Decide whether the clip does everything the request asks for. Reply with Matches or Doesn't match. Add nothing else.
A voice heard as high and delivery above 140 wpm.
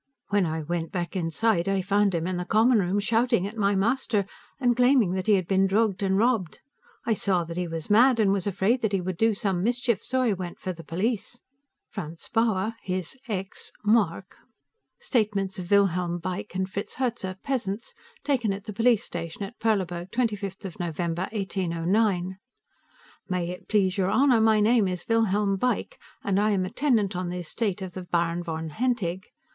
Matches